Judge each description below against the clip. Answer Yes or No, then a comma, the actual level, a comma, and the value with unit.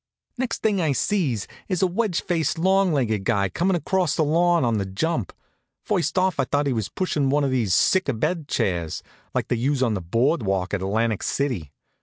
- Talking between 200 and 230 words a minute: Yes, fast, 205 wpm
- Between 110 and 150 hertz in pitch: Yes, medium, 140 Hz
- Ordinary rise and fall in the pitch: No, wide, 8.1 semitones